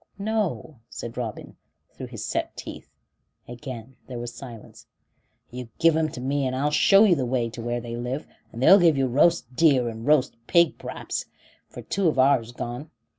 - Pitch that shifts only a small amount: No, average, 4.5 semitones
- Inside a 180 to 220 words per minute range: Yes, average, 190 wpm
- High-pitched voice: No, low, 130 Hz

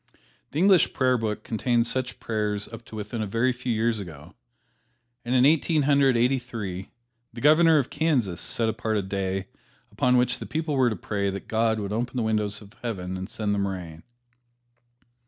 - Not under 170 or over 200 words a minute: Yes, average, 190 wpm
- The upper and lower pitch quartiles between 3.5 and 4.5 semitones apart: Yes, average, 3.9 semitones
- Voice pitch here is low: Yes, low, 115 Hz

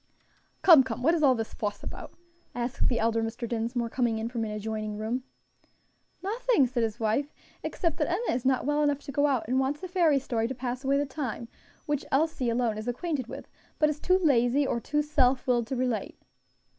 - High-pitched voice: Yes, very high, 255 Hz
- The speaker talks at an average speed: No, fast, 210 wpm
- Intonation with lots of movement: No, average, 4.1 semitones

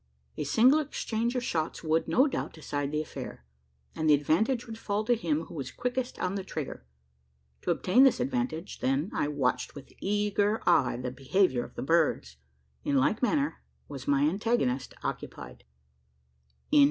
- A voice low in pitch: No, medium, 165 Hz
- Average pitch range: No, wide, 8.2 semitones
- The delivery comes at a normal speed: Yes, average, 165 wpm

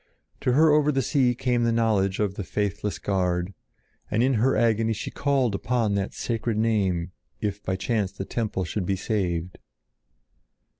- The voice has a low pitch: Yes, low, 110 Hz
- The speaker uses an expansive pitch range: No, average, 3.7 semitones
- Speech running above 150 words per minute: Yes, average, 165 wpm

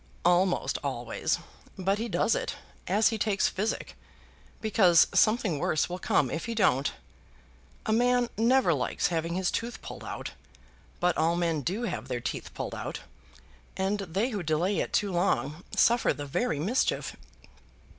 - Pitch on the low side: No, high, 190 Hz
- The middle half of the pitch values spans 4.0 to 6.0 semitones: Yes, average, 5.1 semitones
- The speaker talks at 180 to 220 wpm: No, average, 155 wpm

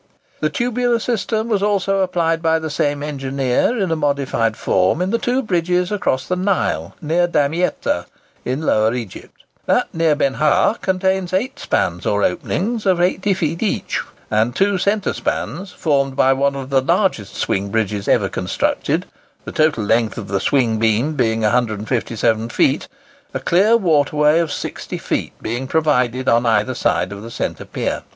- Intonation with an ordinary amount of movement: No, wide, 7.8 semitones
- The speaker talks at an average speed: Yes, average, 160 wpm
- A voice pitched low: No, medium, 150 Hz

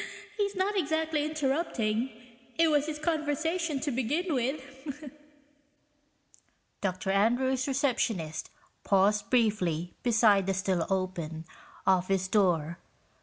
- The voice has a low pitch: No, high, 245 Hz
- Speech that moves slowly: Yes, slow, 100 wpm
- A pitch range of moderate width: No, wide, 7.8 semitones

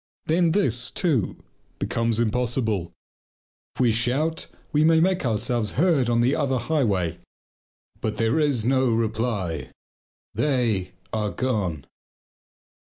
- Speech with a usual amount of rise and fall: Yes, average, 4.7 semitones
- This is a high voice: No, low, 120 Hz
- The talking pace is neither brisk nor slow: No, slow, 115 wpm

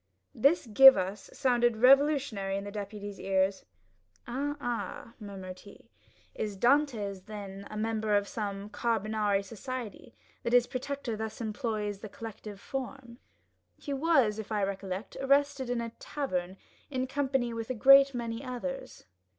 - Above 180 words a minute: No, average, 140 wpm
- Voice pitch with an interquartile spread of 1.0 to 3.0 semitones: No, average, 4.5 semitones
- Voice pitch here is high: Yes, high, 225 Hz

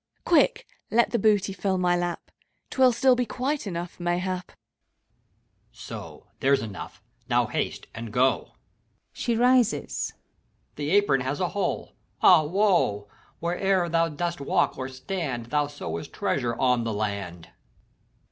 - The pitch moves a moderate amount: No, wide, 7.5 semitones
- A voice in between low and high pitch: Yes, medium, 175 Hz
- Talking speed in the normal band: Yes, average, 145 wpm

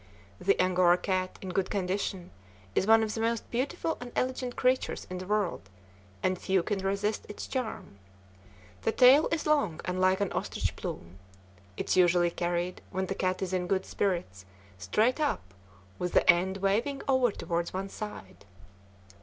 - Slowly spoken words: No, average, 170 wpm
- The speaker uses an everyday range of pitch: Yes, average, 3.8 semitones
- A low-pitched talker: No, high, 190 Hz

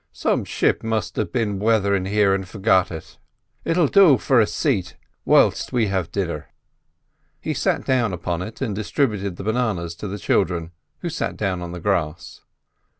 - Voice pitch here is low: Yes, low, 100 Hz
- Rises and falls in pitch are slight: No, average, 3.7 semitones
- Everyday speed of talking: Yes, average, 170 wpm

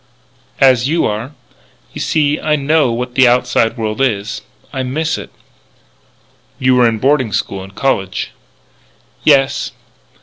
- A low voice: Yes, low, 130 Hz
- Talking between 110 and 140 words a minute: Yes, slow, 135 wpm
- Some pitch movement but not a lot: Yes, average, 3.8 semitones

